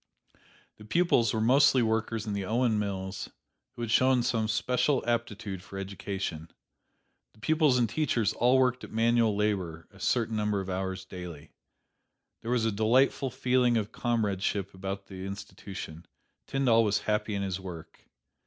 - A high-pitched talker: No, low, 110 Hz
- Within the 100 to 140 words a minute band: No, average, 155 wpm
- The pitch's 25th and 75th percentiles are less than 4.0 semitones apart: Yes, average, 3.6 semitones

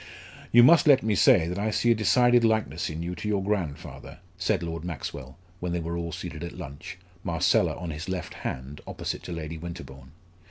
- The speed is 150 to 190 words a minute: No, average, 200 wpm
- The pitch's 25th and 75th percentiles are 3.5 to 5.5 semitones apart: Yes, average, 4.9 semitones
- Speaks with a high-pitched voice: No, very low, 85 Hz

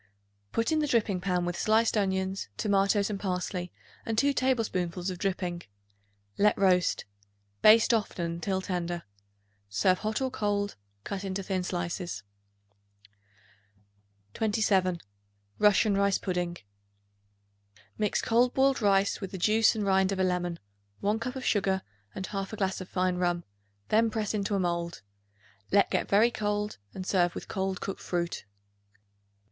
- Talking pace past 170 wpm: No, average, 145 wpm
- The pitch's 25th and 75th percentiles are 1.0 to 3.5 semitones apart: Yes, average, 2.8 semitones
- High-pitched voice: Yes, high, 195 Hz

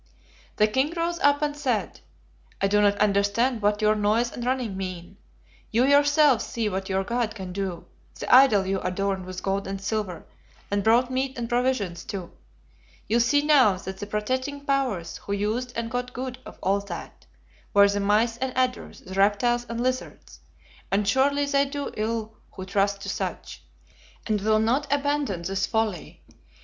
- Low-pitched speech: No, high, 220 Hz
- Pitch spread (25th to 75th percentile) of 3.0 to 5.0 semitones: Yes, average, 4.5 semitones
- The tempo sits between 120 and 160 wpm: No, average, 175 wpm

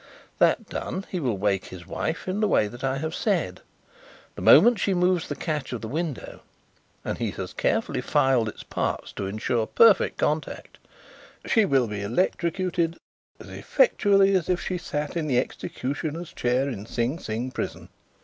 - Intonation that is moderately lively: No, wide, 7.1 semitones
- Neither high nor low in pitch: Yes, medium, 150 Hz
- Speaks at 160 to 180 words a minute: Yes, average, 170 wpm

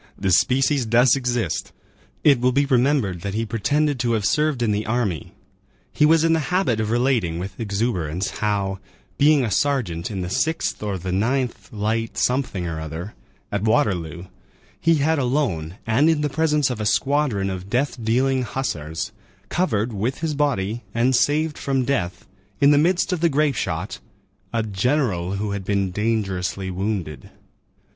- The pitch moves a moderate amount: No, wide, 6.2 semitones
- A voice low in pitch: Yes, low, 115 Hz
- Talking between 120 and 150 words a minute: No, average, 165 wpm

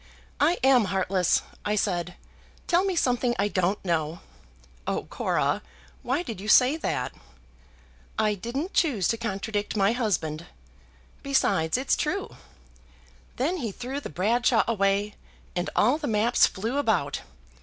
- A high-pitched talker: Yes, high, 220 Hz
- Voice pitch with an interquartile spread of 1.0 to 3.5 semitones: No, average, 5.1 semitones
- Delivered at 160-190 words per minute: No, slow, 135 wpm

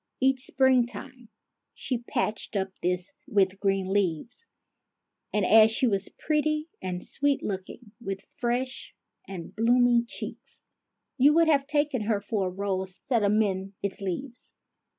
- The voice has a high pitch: Yes, high, 220 Hz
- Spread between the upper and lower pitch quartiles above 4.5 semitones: Yes, average, 5.0 semitones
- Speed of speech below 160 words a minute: Yes, slow, 135 wpm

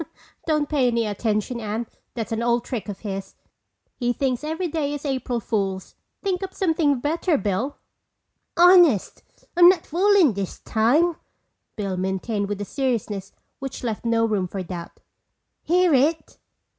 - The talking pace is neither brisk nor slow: Yes, average, 150 wpm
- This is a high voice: Yes, high, 245 Hz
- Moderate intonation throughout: No, wide, 6.8 semitones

